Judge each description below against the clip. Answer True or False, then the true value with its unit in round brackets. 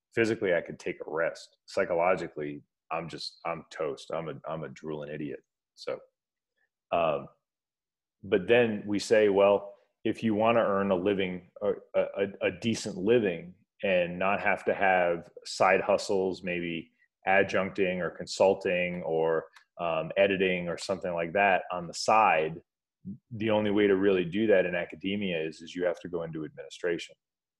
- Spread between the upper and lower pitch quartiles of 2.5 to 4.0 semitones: False (4.4 semitones)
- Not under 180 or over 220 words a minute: False (160 wpm)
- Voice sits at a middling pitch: False (100 Hz)